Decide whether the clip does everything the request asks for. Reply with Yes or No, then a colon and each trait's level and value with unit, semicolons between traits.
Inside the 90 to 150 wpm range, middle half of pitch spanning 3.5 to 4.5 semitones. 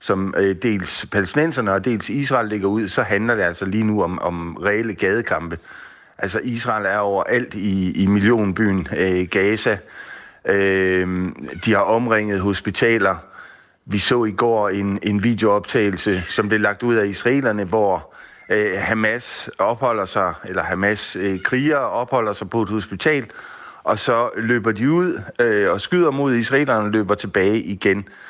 No: slow, 145 wpm; average, 2.8 semitones